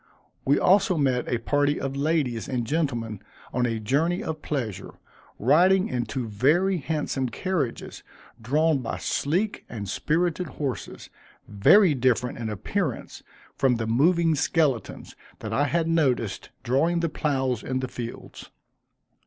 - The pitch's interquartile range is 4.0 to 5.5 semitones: Yes, average, 5.2 semitones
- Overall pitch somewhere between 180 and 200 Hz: No, medium, 140 Hz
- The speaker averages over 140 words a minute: No, slow, 135 wpm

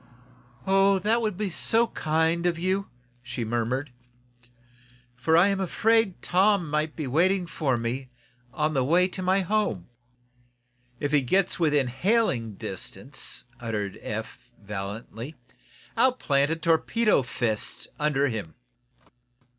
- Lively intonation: Yes, wide, 7.5 semitones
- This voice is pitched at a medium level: Yes, medium, 155 Hz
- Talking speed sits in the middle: No, slow, 130 wpm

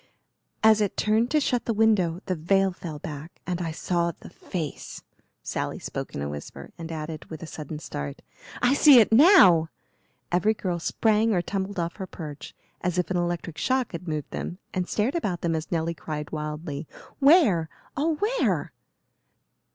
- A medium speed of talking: Yes, average, 175 wpm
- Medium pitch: Yes, medium, 175 Hz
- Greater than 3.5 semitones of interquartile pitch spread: Yes, average, 5.2 semitones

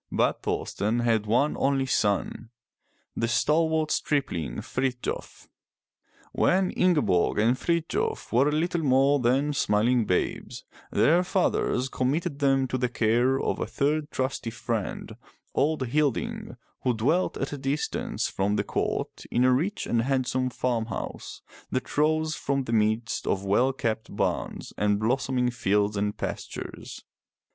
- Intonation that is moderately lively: Yes, average, 4.4 semitones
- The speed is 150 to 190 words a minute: No, slow, 135 wpm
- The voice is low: Yes, low, 130 Hz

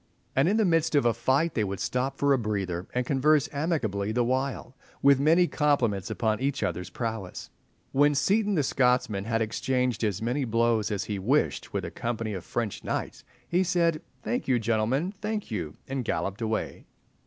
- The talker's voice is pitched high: No, low, 125 Hz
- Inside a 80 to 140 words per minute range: No, average, 185 wpm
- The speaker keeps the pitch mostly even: No, average, 5.1 semitones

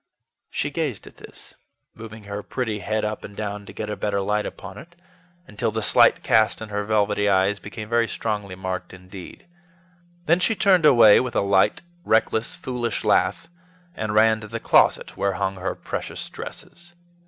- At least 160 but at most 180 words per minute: Yes, average, 175 wpm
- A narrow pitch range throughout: Yes, narrow, 2.3 semitones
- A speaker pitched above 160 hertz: No, low, 105 Hz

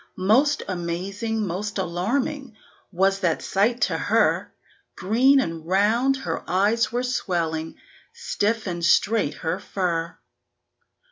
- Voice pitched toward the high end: Yes, high, 200 Hz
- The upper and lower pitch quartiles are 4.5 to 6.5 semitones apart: Yes, average, 5.2 semitones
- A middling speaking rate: No, slow, 115 wpm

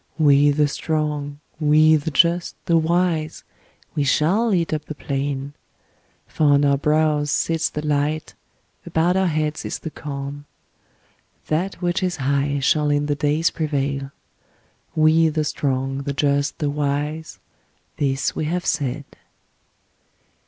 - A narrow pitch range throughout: Yes, narrow, 2.0 semitones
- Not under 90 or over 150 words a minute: Yes, average, 140 wpm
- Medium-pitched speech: Yes, medium, 150 Hz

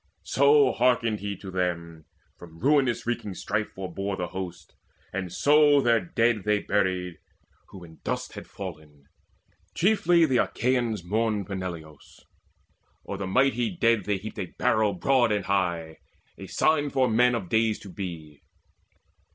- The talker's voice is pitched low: Yes, low, 105 Hz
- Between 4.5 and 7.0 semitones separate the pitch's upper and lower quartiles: Yes, average, 5.2 semitones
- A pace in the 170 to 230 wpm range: No, average, 145 wpm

